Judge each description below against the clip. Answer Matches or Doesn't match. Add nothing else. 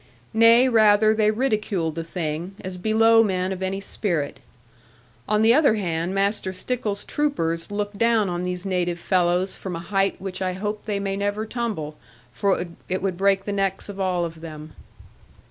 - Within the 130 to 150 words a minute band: Doesn't match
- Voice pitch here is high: Matches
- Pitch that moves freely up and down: Doesn't match